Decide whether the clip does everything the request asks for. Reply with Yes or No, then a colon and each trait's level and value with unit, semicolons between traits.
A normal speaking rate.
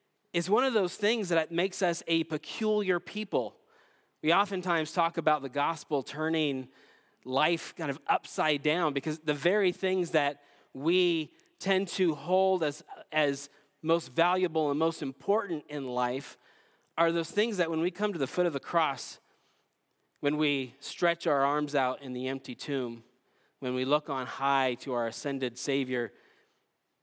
Yes: average, 160 wpm